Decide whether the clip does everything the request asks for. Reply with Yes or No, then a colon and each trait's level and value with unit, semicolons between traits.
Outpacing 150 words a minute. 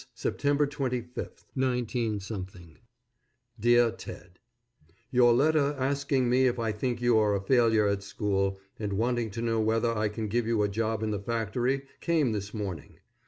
Yes: average, 165 wpm